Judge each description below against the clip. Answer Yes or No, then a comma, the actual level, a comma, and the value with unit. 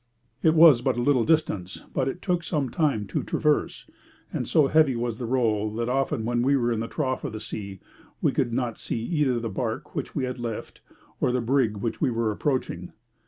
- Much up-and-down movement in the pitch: No, average, 3.8 semitones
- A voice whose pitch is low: Yes, low, 125 Hz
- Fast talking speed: Yes, fast, 215 wpm